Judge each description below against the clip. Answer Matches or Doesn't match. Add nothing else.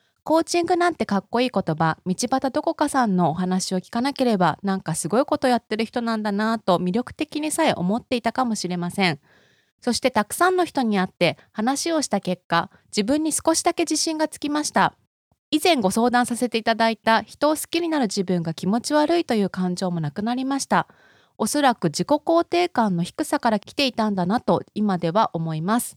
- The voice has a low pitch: Doesn't match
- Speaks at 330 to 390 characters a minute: Doesn't match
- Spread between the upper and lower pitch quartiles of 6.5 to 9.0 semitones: Matches